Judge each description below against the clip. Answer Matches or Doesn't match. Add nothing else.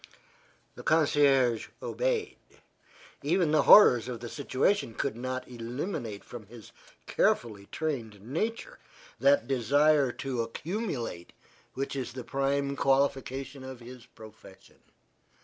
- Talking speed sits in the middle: Doesn't match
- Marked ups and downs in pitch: Doesn't match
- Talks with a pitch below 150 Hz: Matches